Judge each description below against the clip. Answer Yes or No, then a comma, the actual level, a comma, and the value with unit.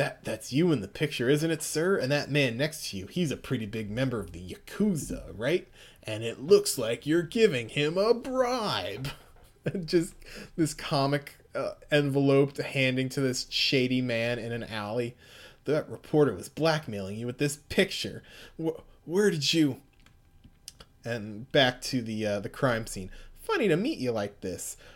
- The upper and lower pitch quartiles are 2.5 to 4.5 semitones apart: No, average, 5.3 semitones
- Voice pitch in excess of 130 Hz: Yes, medium, 140 Hz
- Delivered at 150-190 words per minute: Yes, average, 175 wpm